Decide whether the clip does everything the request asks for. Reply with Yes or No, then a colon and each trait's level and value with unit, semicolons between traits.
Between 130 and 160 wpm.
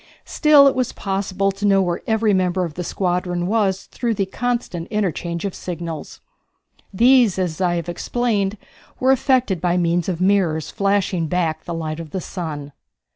No: average, 170 wpm